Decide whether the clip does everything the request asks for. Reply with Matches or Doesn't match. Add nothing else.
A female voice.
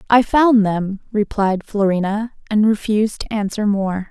Matches